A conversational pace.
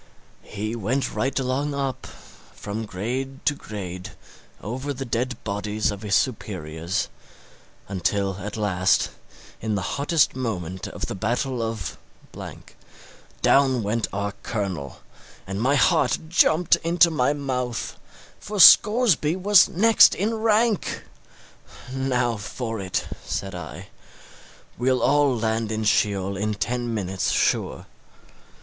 No: slow, 120 wpm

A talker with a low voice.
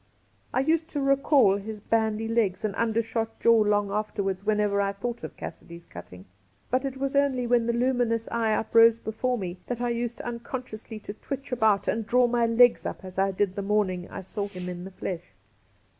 No: high, 225 Hz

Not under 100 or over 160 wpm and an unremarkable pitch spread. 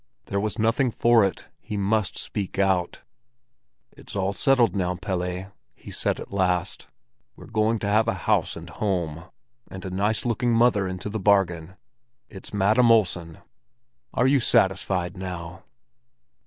Yes: average, 150 wpm; average, 3.2 semitones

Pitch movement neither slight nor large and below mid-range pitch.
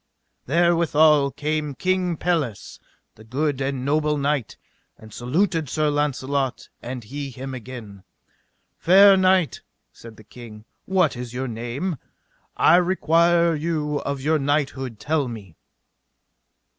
No: average, 4.5 semitones; medium, 145 Hz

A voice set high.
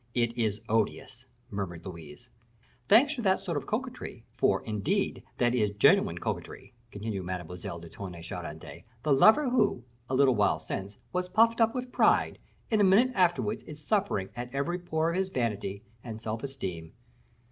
No: low, 120 Hz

